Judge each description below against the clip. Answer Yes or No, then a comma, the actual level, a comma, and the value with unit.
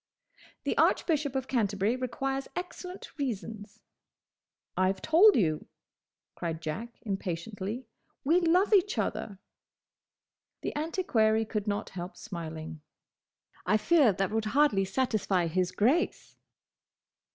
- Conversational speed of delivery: No, slow, 110 wpm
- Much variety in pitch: Yes, wide, 6.7 semitones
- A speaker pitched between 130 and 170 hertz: No, high, 220 Hz